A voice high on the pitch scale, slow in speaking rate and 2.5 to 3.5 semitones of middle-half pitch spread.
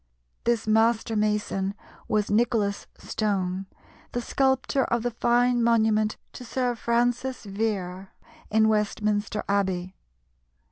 Yes: high, 220 Hz; slow, 105 wpm; average, 2.8 semitones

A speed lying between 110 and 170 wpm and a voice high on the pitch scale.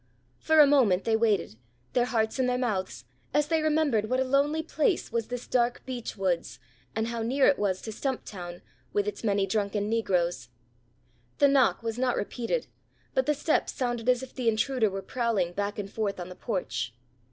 No: average, 190 wpm; high, 230 Hz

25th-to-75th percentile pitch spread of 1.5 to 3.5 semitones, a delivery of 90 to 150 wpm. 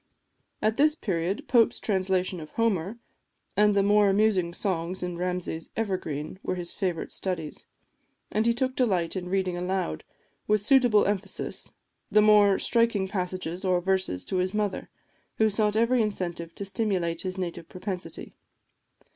Yes: average, 2.9 semitones; average, 145 wpm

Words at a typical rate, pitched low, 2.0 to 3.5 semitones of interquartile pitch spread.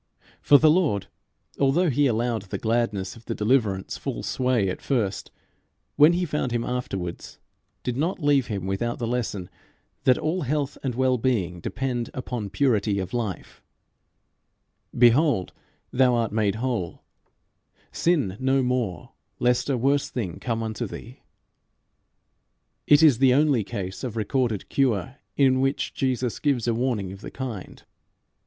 No: average, 150 wpm; low, 125 Hz; average, 4.0 semitones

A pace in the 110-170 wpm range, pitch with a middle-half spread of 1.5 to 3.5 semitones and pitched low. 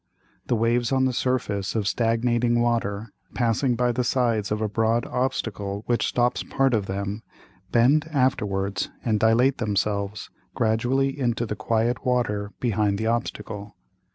Yes: average, 145 wpm; average, 2.8 semitones; low, 115 Hz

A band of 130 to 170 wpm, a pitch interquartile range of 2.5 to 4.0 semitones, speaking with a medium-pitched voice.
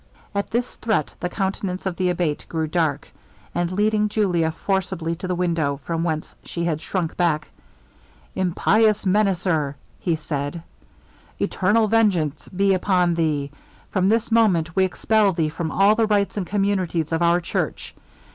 Yes: average, 155 wpm; average, 3.6 semitones; medium, 180 Hz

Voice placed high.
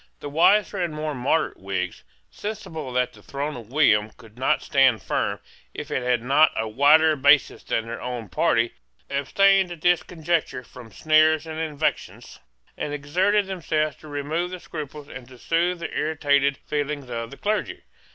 No: medium, 150 Hz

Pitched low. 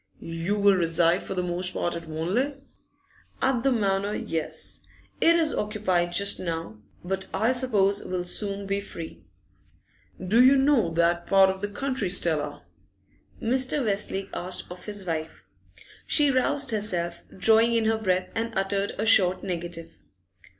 No: high, 195 Hz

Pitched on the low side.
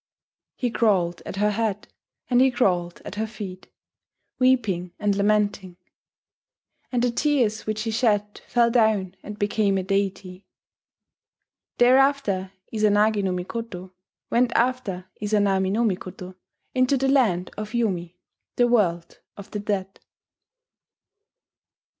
No: high, 210 Hz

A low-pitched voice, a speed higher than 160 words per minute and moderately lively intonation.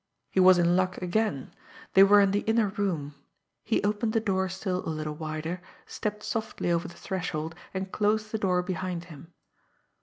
No: medium, 185 Hz; average, 180 wpm; average, 3.3 semitones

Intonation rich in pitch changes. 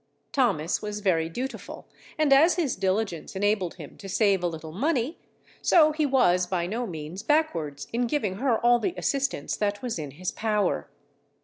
Yes: wide, 6.9 semitones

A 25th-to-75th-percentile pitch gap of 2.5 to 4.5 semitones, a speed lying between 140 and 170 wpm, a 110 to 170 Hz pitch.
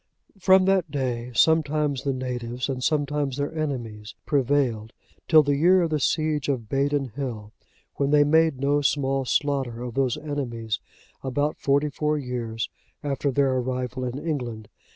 Yes: average, 2.9 semitones; average, 150 wpm; medium, 140 Hz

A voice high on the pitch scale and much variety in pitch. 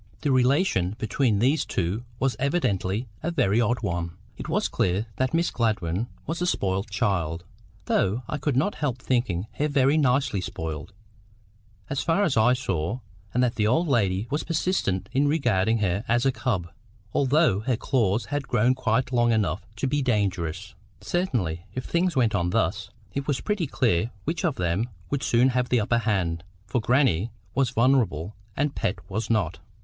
No: low, 120 Hz; wide, 5.7 semitones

